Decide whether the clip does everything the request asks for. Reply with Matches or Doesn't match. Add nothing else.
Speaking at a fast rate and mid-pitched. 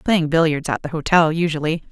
Doesn't match